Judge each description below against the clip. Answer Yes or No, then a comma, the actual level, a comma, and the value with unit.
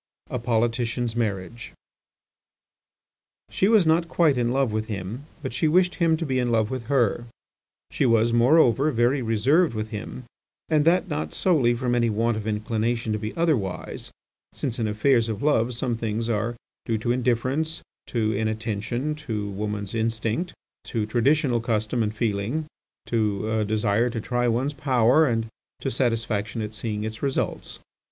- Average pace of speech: Yes, average, 160 wpm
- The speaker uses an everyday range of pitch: Yes, average, 3.3 semitones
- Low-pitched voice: Yes, low, 115 Hz